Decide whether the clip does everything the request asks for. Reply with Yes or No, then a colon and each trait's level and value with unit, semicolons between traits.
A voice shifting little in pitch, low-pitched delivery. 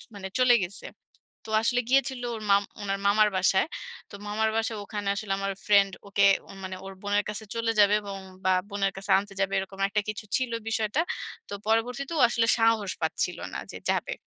No: narrow, 2.3 semitones; high, 205 Hz